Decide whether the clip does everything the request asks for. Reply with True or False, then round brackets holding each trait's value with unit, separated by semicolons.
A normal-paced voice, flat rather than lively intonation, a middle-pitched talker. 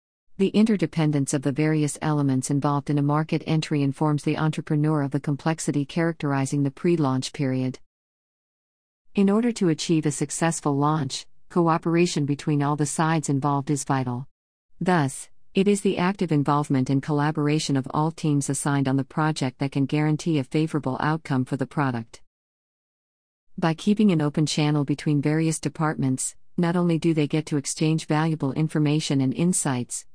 True (160 wpm; 2.3 semitones; 150 Hz)